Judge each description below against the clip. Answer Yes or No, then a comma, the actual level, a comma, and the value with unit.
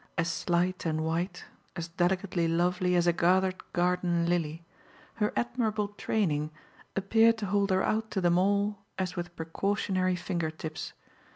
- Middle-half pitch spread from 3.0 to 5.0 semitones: No, narrow, 2.6 semitones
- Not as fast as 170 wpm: Yes, average, 150 wpm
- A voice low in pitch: No, medium, 180 Hz